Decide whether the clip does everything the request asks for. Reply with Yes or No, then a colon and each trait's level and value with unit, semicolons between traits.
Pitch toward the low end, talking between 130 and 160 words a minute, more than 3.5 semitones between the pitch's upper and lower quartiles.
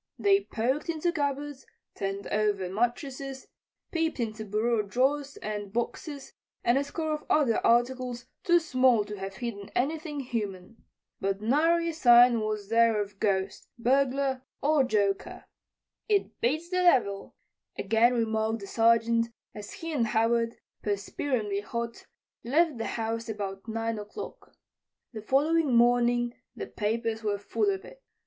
No: high, 235 Hz; average, 140 wpm; average, 4.6 semitones